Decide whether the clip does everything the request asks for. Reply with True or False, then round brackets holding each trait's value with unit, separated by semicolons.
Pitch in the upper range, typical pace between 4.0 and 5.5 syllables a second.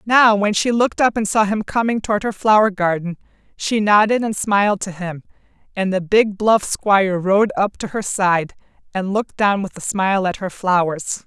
True (200 Hz; 5.0 syllables/s)